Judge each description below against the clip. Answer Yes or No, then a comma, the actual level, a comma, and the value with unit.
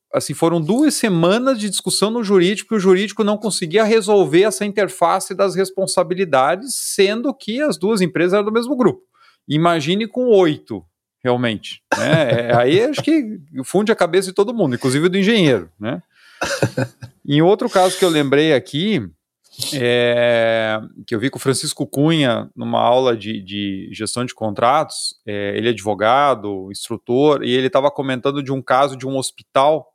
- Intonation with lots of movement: Yes, wide, 8.4 semitones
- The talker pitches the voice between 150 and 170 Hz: Yes, medium, 165 Hz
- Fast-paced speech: No, average, 165 wpm